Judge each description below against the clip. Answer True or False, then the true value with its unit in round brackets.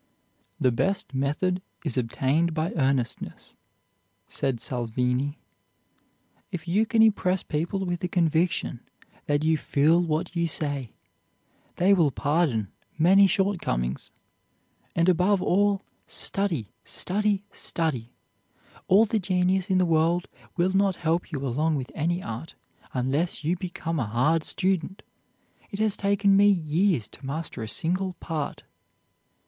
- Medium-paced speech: False (130 wpm)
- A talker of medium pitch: True (165 Hz)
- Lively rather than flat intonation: False (4.9 semitones)